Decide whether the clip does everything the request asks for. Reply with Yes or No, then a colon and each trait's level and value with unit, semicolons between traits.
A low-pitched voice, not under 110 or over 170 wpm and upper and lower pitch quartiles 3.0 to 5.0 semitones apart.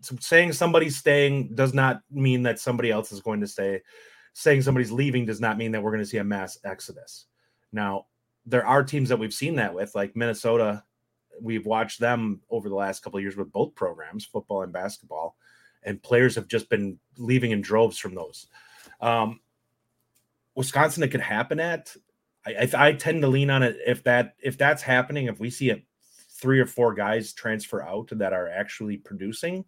No: low, 120 Hz; average, 195 wpm; average, 3.5 semitones